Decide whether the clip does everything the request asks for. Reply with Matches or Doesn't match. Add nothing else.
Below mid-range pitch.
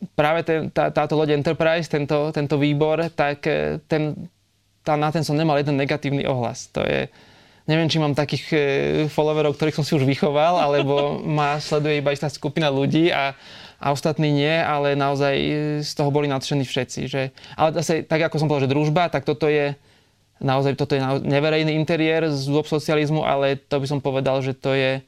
Doesn't match